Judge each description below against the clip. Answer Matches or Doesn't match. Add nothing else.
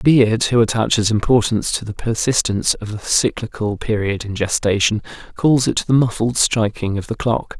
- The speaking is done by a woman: Doesn't match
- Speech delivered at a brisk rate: Doesn't match